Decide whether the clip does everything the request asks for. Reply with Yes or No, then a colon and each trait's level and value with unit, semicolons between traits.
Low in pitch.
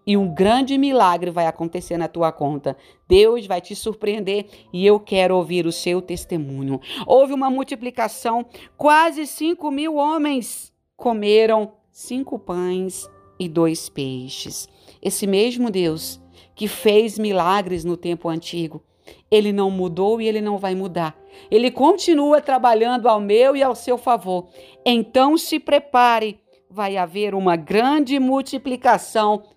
No: high, 210 Hz